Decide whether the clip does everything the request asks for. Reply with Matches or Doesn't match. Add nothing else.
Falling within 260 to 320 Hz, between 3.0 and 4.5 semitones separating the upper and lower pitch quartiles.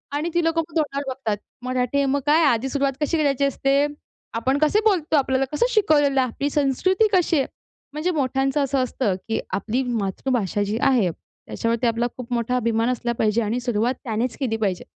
Matches